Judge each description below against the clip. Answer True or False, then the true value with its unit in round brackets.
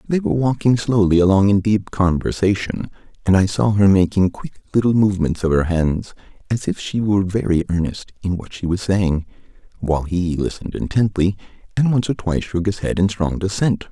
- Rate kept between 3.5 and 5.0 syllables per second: False (5.5 syllables/s)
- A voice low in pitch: True (95 Hz)